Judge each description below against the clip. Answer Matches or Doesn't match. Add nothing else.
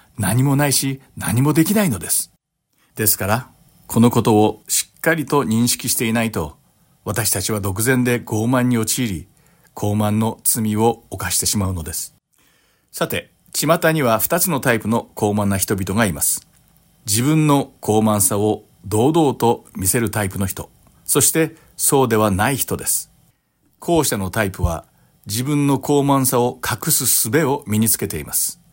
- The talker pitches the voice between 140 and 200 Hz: Doesn't match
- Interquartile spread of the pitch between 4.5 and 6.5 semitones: Matches